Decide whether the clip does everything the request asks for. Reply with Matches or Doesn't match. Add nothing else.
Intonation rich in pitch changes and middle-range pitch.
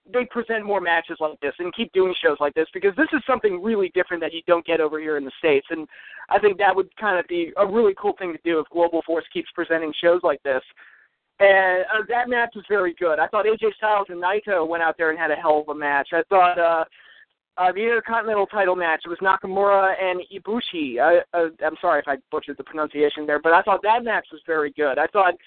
Doesn't match